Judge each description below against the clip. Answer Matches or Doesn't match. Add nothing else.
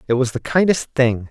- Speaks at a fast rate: Matches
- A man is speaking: Matches